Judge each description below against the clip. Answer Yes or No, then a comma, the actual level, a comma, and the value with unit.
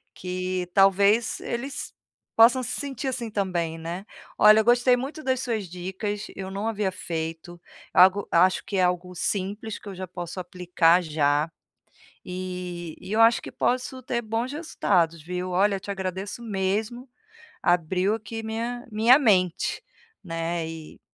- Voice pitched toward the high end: Yes, high, 195 Hz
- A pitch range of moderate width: Yes, average, 4.0 semitones